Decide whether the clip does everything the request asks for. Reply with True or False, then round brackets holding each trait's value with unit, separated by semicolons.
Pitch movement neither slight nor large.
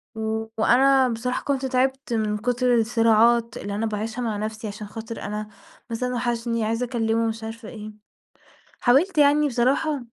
False (2.3 semitones)